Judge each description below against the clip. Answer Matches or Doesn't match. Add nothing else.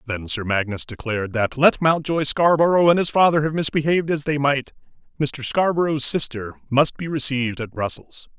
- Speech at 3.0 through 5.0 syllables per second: Doesn't match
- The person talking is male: Matches